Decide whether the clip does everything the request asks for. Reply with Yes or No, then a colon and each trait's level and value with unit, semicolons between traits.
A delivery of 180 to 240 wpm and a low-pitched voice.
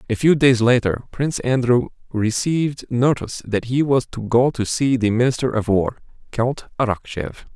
No: average, 165 wpm; low, 120 Hz